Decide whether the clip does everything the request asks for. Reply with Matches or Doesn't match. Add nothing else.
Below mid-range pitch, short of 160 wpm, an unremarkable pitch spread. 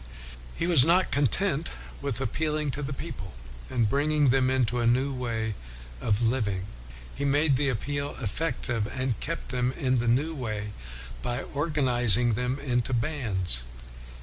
Matches